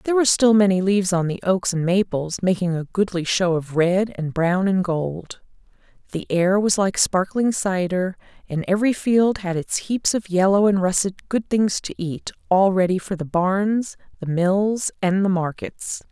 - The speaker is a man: No, female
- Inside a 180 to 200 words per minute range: Yes, average, 185 wpm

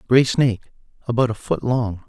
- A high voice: No, low, 120 Hz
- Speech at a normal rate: Yes, average, 175 wpm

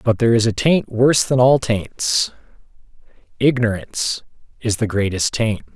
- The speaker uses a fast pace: No, slow, 135 wpm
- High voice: No, low, 115 Hz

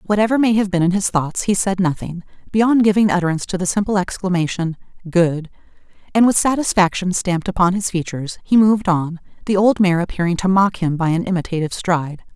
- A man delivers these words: No, female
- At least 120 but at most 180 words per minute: No, average, 190 wpm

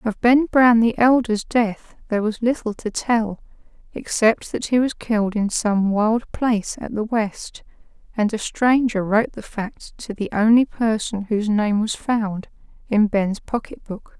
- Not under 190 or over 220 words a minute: No, average, 175 wpm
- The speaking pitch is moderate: No, high, 220 Hz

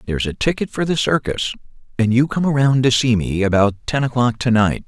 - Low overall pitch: Yes, low, 120 Hz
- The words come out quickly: Yes, fast, 220 wpm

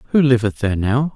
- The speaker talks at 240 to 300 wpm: No, fast, 205 wpm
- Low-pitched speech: Yes, low, 125 Hz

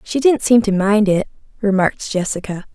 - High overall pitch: Yes, high, 210 Hz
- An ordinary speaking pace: Yes, average, 175 wpm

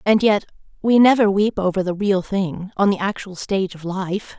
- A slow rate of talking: No, fast, 205 wpm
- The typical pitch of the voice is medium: No, high, 195 Hz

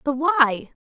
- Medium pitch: No, very high, 285 Hz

